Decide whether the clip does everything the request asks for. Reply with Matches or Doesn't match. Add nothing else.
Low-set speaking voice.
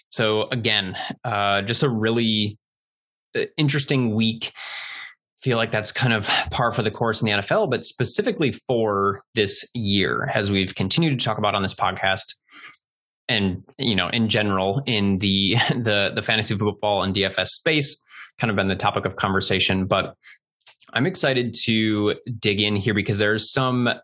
Matches